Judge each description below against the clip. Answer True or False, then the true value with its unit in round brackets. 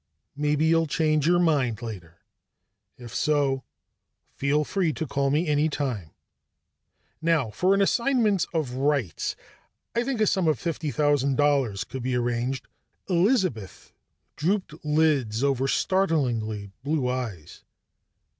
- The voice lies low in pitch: False (145 Hz)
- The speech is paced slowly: True (130 wpm)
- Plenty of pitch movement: False (4.7 semitones)